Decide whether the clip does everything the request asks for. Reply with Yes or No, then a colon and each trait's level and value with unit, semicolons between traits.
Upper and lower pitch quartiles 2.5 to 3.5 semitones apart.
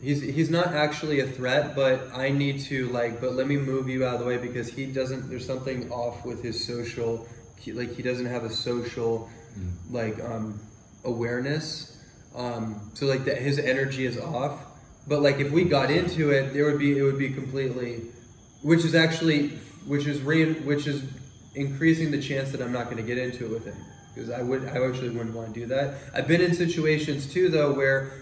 Yes: average, 3.1 semitones